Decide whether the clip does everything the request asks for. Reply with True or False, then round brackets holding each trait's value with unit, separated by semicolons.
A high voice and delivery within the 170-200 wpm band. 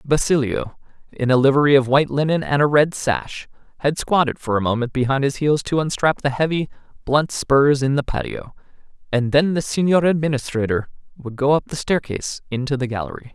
False (140 Hz; 185 wpm)